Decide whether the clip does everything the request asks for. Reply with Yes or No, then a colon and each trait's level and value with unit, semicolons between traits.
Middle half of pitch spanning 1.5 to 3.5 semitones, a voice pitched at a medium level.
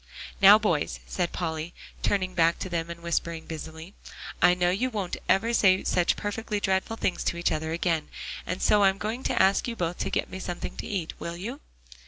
Yes: average, 3.2 semitones; medium, 180 Hz